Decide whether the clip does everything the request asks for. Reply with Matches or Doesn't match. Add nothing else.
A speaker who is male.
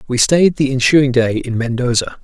Matches